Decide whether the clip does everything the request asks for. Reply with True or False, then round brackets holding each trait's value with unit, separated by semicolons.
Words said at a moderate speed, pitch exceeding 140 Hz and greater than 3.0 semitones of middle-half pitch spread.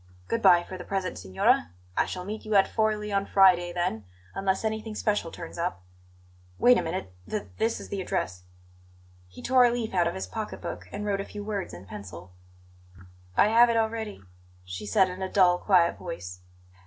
True (195 wpm; 190 Hz; 4.3 semitones)